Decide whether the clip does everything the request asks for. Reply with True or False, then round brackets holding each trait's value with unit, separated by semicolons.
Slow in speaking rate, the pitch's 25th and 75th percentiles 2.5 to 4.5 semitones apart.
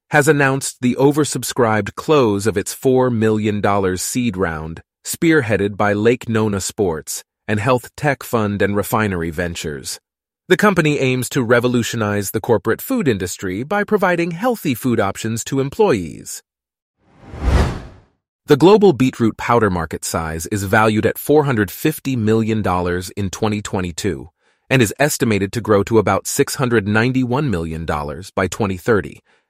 False (130 wpm; 4.9 semitones)